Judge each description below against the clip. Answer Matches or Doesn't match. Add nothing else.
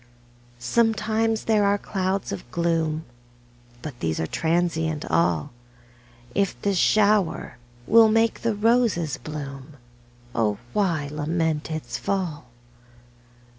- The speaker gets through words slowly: Matches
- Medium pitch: Matches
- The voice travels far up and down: Matches